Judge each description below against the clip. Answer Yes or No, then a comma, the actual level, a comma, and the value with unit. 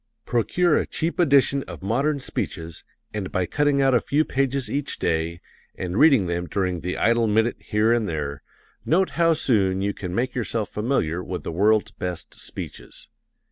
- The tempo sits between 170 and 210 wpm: Yes, average, 175 wpm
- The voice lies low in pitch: Yes, low, 110 Hz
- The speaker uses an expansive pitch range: Yes, wide, 7.1 semitones